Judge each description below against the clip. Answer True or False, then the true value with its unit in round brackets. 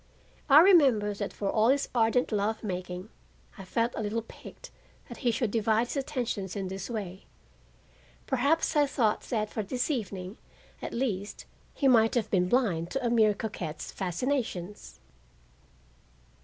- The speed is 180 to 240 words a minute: False (155 wpm)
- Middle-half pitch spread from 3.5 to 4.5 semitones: True (4.1 semitones)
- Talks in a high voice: True (220 Hz)